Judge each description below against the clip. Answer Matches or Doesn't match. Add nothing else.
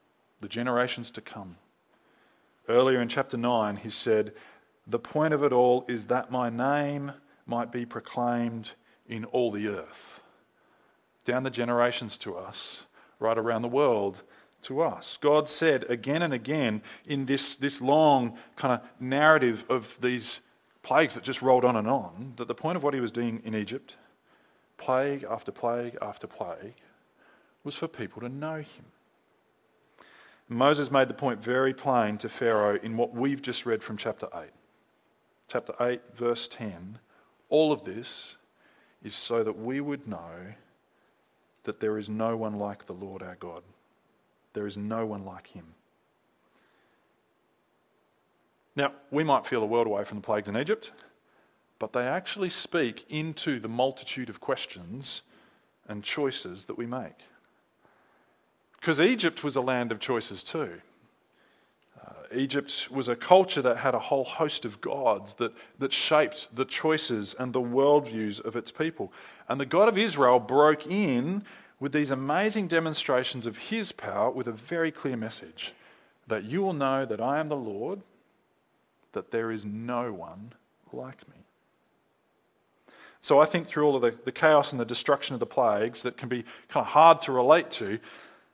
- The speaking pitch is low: Matches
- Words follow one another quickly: Doesn't match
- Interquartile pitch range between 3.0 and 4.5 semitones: Matches